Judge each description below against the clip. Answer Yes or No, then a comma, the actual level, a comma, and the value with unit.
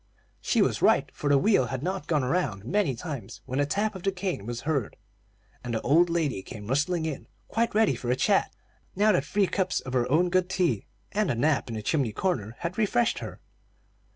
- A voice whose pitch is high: No, medium, 155 Hz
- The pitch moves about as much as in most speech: No, wide, 6.9 semitones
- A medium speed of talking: No, fast, 215 wpm